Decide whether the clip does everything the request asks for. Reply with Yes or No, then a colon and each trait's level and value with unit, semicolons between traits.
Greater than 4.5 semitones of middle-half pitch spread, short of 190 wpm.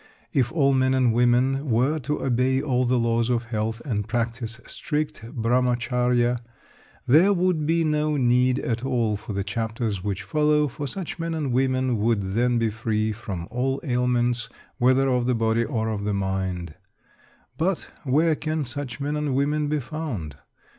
No: average, 3.9 semitones; average, 165 wpm